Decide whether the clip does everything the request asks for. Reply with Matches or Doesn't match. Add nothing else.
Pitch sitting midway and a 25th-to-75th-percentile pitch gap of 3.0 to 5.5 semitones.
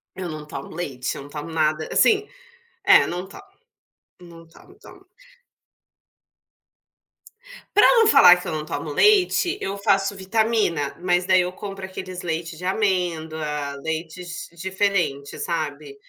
Matches